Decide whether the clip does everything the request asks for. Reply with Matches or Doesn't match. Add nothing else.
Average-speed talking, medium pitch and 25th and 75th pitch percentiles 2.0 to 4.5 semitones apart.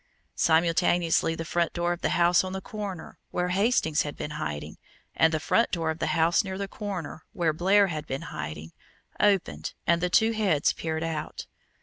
Matches